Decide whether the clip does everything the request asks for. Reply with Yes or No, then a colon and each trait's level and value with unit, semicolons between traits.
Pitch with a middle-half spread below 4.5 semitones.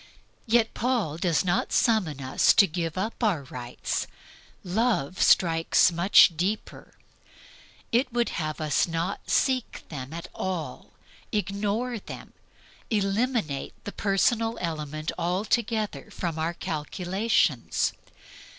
No: wide, 5.5 semitones